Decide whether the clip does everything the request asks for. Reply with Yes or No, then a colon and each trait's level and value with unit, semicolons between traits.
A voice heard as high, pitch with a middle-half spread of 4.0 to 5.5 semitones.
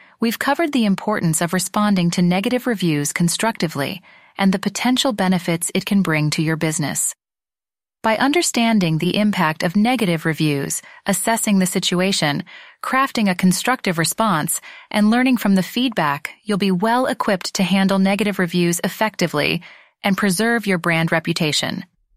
Yes: high, 195 Hz; average, 4.4 semitones